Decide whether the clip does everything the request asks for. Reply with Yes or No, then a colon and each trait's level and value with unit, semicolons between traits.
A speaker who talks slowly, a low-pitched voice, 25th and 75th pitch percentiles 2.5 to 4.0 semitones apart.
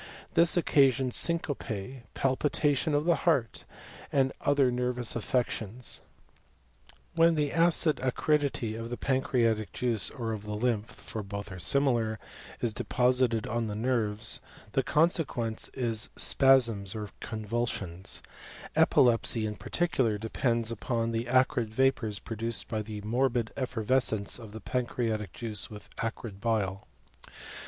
Yes: slow, 130 wpm; low, 115 Hz; average, 3.3 semitones